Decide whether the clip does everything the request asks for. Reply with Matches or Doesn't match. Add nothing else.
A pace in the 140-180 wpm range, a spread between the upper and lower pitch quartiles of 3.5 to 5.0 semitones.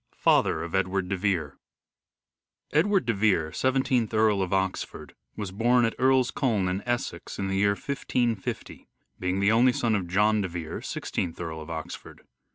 Matches